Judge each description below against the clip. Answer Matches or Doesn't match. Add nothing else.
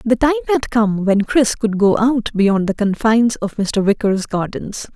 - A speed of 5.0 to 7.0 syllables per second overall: Doesn't match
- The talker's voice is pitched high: Matches